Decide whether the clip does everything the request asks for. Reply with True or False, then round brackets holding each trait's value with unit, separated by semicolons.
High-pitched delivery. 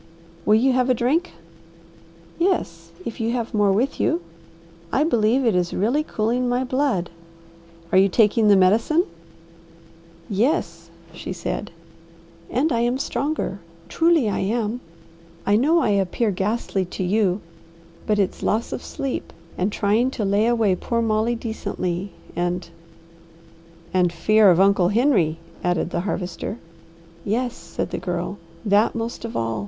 True (215 Hz)